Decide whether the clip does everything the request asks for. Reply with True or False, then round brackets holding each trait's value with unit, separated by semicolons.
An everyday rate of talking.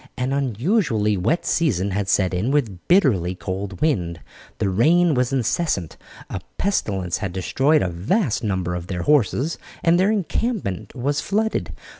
True (150 wpm)